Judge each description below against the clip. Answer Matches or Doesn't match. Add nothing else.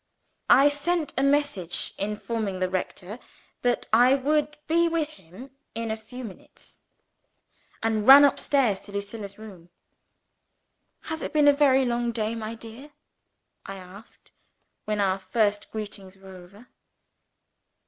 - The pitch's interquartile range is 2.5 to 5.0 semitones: Doesn't match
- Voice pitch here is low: Doesn't match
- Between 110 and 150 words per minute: Matches